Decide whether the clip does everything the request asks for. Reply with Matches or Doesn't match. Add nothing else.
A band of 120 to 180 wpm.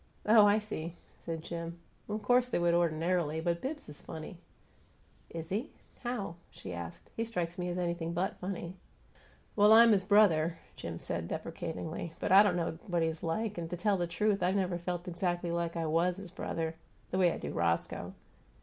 Doesn't match